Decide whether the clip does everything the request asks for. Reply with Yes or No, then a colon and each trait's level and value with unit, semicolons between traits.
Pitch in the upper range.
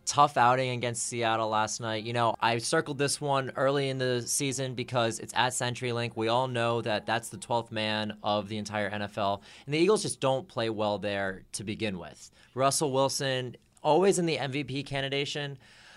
No: low, 120 Hz